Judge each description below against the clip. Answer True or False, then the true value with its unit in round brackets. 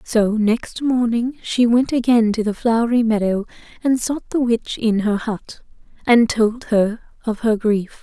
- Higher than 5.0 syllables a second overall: False (4.1 syllables/s)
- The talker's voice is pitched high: True (230 Hz)